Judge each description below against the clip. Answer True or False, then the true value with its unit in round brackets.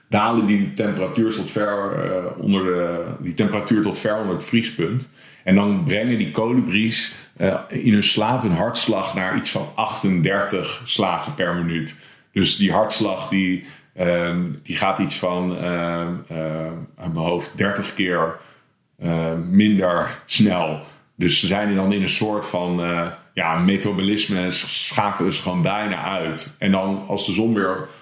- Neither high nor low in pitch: False (95 Hz)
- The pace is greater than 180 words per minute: False (165 wpm)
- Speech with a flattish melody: False (3.3 semitones)